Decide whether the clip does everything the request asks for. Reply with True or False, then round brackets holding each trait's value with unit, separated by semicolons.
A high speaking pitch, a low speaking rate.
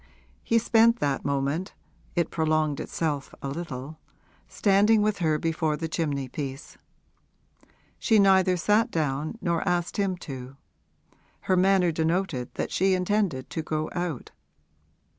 False (165 Hz; 130 wpm)